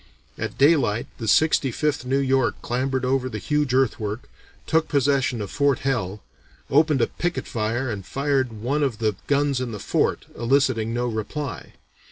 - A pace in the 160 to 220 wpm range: Yes, average, 165 wpm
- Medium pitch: No, low, 130 Hz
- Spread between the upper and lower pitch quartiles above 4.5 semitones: No, average, 3.7 semitones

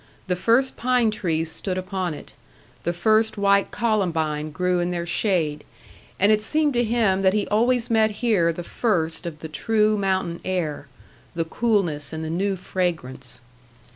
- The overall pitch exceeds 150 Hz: Yes, medium, 185 Hz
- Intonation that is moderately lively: Yes, average, 4.7 semitones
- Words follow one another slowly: No, average, 165 wpm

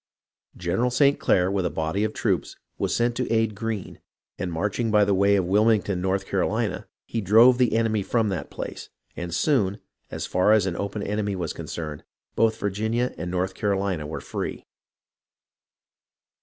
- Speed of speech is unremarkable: Yes, average, 170 wpm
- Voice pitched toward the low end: Yes, low, 100 Hz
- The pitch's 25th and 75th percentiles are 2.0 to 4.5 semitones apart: Yes, average, 3.2 semitones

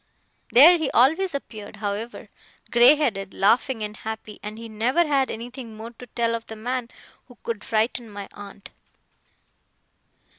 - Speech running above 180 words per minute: No, average, 150 wpm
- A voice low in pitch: No, high, 230 Hz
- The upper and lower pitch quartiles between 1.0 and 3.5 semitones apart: Yes, average, 3.0 semitones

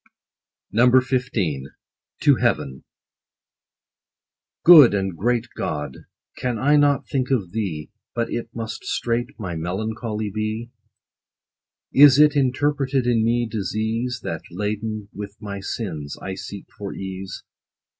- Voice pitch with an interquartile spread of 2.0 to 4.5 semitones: Yes, average, 4.2 semitones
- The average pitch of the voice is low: Yes, low, 110 Hz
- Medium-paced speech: No, slow, 125 wpm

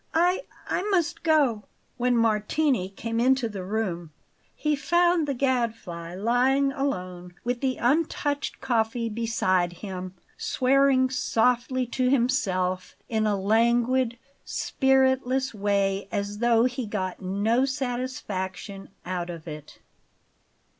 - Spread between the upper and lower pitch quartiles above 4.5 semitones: Yes, average, 5.1 semitones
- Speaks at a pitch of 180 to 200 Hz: No, high, 235 Hz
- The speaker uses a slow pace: Yes, slow, 115 wpm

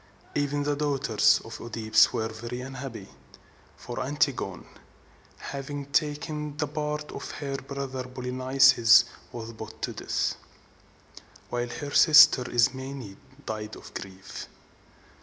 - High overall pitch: No, low, 130 Hz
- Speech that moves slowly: Yes, slow, 115 wpm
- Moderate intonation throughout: Yes, average, 3.5 semitones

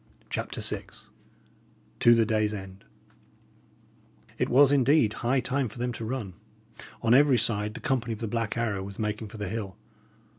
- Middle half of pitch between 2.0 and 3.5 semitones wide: Yes, average, 2.8 semitones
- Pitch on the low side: Yes, low, 115 Hz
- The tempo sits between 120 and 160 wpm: No, average, 170 wpm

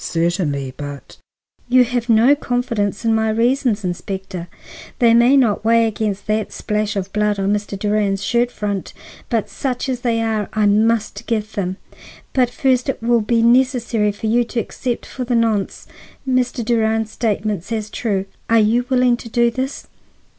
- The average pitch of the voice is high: Yes, high, 225 Hz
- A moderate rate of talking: Yes, average, 170 wpm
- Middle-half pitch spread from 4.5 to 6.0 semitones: No, average, 2.8 semitones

